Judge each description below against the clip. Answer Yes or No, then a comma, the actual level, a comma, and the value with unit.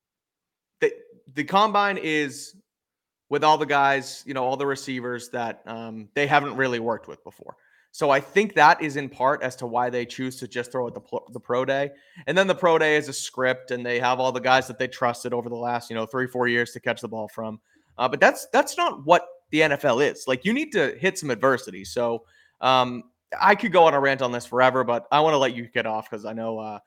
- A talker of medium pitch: No, low, 130 Hz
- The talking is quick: Yes, fast, 245 wpm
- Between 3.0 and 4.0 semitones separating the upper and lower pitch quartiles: Yes, average, 3.6 semitones